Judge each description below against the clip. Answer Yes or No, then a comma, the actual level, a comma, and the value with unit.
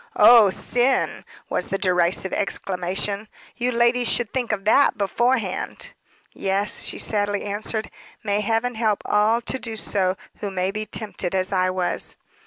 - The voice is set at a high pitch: Yes, high, 210 Hz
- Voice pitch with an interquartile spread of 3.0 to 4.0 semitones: Yes, average, 3.3 semitones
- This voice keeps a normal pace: Yes, average, 150 wpm